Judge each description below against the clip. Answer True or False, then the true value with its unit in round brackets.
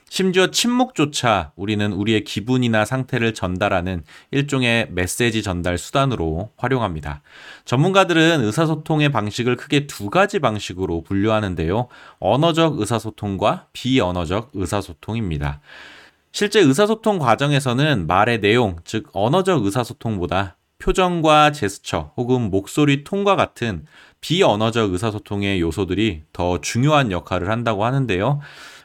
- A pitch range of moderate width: False (6.5 semitones)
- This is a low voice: True (115 Hz)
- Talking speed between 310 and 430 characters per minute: True (320 characters per minute)